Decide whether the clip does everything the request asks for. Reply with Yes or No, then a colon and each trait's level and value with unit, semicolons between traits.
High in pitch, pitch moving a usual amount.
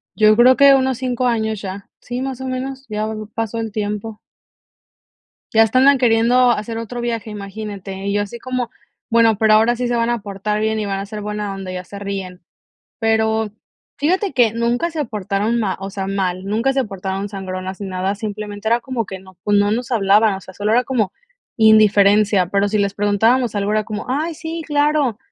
Yes: high, 215 Hz; average, 3.1 semitones